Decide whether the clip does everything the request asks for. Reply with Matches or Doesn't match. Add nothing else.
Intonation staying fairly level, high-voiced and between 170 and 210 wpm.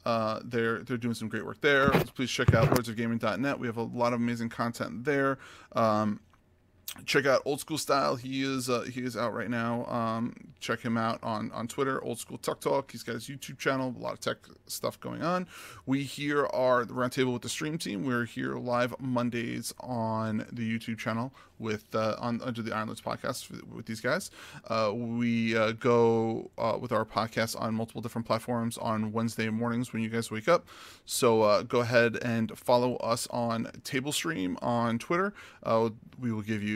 Doesn't match